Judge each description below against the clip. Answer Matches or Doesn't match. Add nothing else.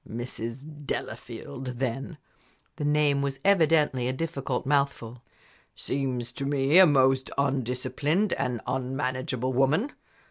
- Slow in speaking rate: Matches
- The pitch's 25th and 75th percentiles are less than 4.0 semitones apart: Matches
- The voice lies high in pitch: Doesn't match